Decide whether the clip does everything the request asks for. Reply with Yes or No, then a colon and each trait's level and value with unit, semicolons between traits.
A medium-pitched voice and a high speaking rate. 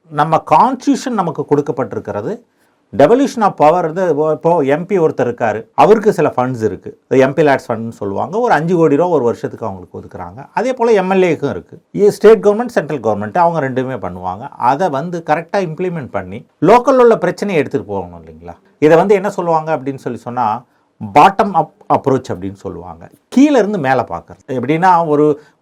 Yes: medium, 155 Hz; fast, 160 wpm